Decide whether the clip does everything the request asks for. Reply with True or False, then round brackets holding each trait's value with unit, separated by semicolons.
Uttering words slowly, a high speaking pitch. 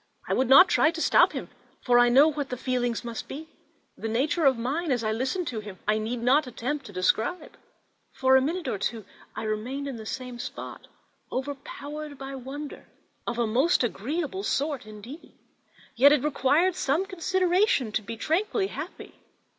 False (180 wpm; 265 Hz)